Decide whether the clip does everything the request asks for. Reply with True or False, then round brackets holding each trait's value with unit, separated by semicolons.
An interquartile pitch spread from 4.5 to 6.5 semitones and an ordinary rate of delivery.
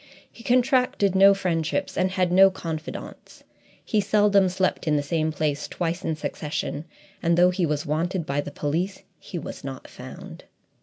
False (3.8 semitones; 165 wpm)